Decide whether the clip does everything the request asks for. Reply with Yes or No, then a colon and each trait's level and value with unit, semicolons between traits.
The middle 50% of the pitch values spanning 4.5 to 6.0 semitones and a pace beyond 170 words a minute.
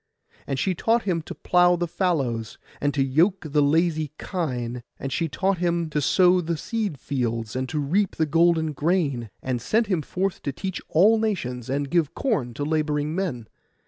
Yes: average, 4.8 semitones; average, 185 wpm